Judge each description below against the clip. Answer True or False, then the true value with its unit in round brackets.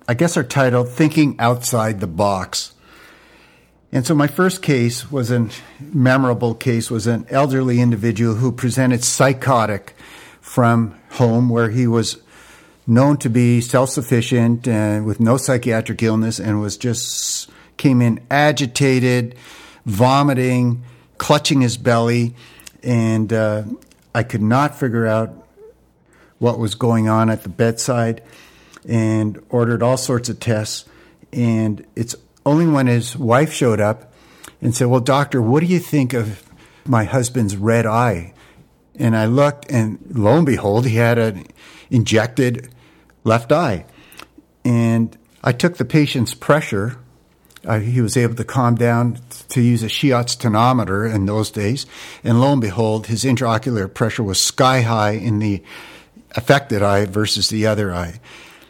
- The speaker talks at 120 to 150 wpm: True (145 wpm)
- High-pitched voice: False (120 Hz)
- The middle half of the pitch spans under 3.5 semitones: True (2.6 semitones)